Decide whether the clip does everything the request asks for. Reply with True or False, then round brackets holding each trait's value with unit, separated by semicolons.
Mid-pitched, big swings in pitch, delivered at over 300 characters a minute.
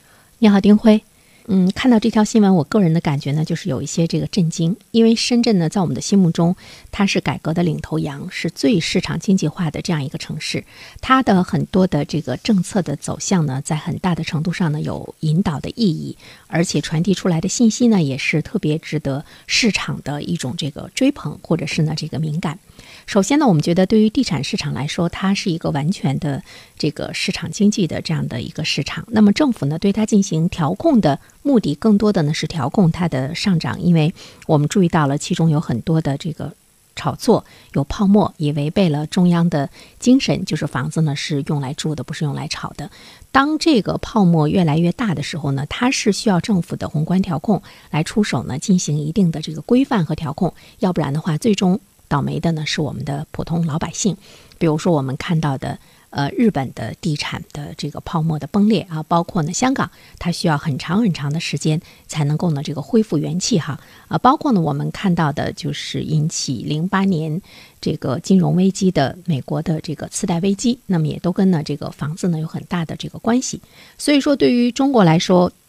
False (170 Hz; 4.5 semitones; 315 characters per minute)